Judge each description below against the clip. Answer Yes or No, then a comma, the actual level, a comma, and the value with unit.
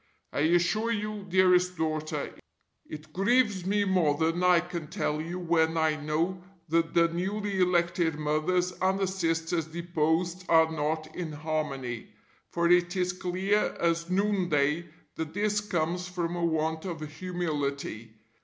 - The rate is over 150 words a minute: No, average, 145 wpm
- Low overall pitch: No, medium, 170 Hz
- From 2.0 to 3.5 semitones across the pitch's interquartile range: Yes, narrow, 2.6 semitones